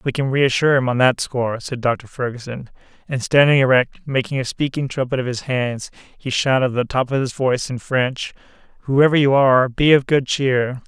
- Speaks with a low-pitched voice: Yes, low, 130 Hz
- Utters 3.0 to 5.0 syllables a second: No, 5.4 syllables/s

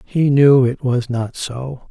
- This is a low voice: Yes, low, 130 Hz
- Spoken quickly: No, average, 190 wpm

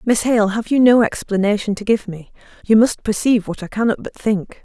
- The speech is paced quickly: Yes, fast, 220 wpm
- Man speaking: No, female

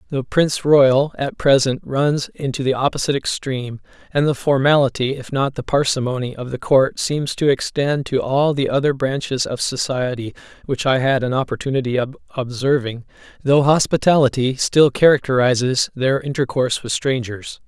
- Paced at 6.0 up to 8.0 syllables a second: No, 5.1 syllables/s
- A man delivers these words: Yes, male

